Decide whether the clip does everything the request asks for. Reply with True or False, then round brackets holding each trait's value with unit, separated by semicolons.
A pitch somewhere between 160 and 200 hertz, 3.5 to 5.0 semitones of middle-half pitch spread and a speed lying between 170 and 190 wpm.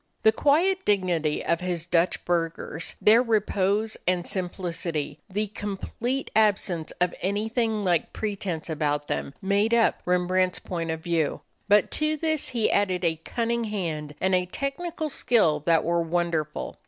False (185 Hz; 4.6 semitones; 145 wpm)